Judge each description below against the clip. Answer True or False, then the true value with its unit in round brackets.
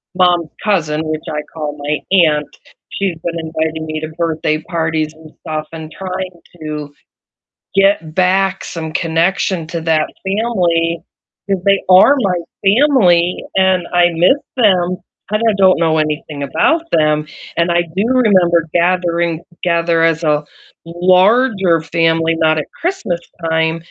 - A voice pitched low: False (170 Hz)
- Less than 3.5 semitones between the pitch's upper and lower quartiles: True (2.8 semitones)